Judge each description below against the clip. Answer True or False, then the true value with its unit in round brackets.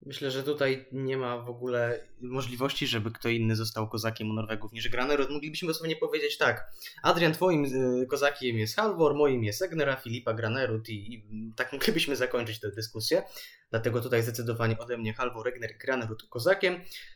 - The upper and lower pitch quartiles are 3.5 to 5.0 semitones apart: True (3.9 semitones)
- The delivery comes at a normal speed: False (165 wpm)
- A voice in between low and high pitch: False (125 Hz)